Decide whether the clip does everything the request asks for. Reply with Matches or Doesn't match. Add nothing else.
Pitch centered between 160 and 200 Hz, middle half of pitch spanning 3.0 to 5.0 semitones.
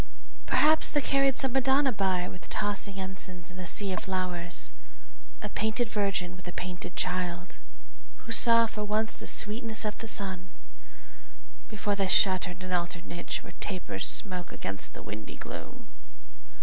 Matches